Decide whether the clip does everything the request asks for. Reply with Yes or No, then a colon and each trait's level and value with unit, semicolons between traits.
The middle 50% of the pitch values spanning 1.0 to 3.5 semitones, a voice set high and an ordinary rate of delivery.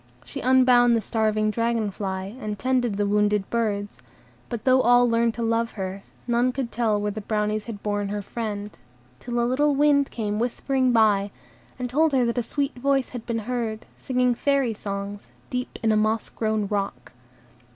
Yes: average, 3.1 semitones; high, 230 Hz; average, 185 wpm